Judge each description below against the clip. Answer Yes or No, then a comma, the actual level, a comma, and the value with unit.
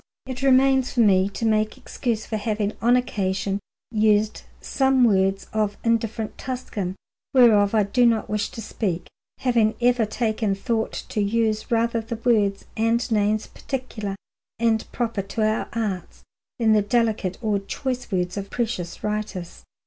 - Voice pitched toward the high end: Yes, high, 220 Hz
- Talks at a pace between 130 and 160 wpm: Yes, average, 150 wpm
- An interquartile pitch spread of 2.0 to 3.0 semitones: Yes, narrow, 2.5 semitones